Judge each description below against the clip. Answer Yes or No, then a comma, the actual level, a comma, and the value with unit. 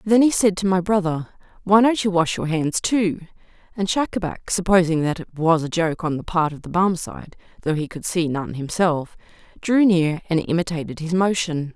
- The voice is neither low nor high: Yes, medium, 175 Hz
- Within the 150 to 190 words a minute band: No, average, 200 wpm